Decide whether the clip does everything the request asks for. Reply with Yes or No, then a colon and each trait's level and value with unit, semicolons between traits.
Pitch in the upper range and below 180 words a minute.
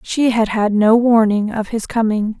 No: high, 220 Hz; average, 200 wpm